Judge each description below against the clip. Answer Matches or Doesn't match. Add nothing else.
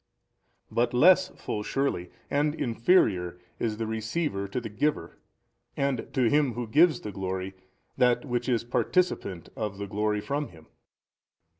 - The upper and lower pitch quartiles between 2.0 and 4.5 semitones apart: Doesn't match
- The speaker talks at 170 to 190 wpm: Doesn't match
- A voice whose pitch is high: Doesn't match